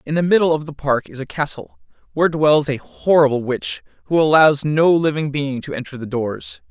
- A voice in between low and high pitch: Yes, medium, 145 Hz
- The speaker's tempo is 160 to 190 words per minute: No, fast, 205 wpm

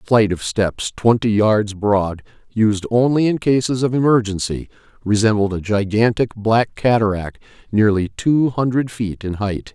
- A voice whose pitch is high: No, low, 110 Hz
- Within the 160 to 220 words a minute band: No, average, 150 wpm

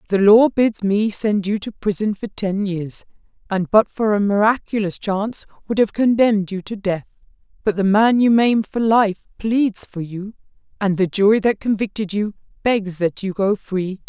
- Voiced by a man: No, female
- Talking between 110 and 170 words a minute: No, average, 190 wpm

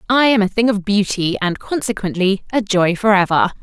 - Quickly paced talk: No, average, 180 wpm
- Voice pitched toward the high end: Yes, high, 205 Hz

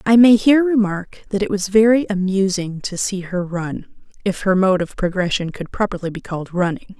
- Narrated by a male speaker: No, female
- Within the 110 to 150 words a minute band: No, average, 195 wpm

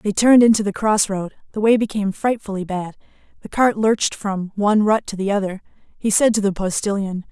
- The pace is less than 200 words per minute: No, fast, 205 wpm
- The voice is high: Yes, high, 205 Hz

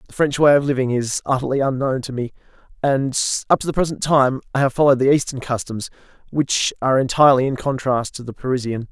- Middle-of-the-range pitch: No, low, 130 Hz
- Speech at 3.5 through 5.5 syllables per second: No, 6.1 syllables/s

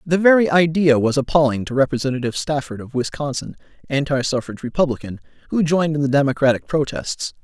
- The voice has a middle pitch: Yes, medium, 145 Hz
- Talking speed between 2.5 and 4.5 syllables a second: No, 6.3 syllables/s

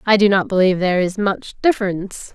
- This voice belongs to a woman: Yes, female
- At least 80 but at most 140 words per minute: No, fast, 205 wpm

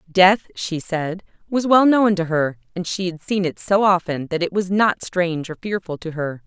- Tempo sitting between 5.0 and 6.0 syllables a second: No, 4.7 syllables/s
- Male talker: No, female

